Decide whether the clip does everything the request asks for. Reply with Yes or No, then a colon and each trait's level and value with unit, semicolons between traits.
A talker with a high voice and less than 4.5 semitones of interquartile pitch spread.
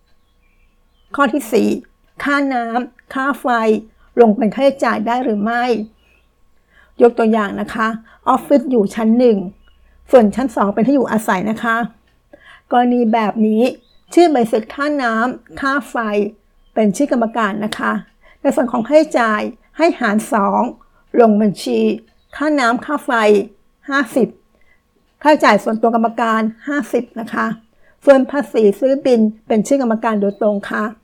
Yes: high, 230 Hz; average, 3.7 semitones